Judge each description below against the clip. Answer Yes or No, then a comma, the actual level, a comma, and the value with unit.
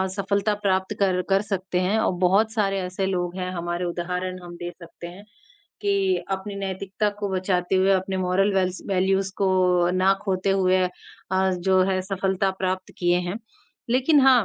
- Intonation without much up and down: Yes, narrow, 1.3 semitones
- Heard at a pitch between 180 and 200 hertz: Yes, high, 190 Hz